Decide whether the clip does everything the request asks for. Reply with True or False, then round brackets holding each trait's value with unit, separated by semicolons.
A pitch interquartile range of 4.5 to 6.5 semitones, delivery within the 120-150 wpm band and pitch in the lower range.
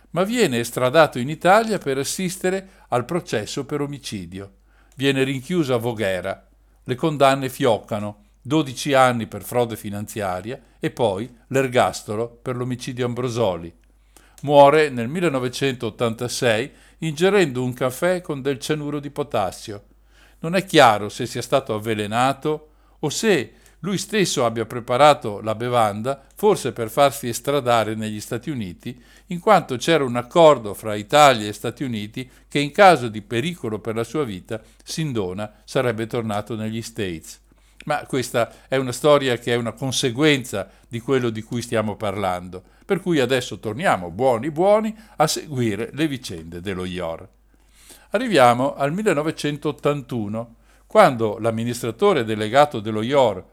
True (4.9 semitones; 135 wpm; 125 Hz)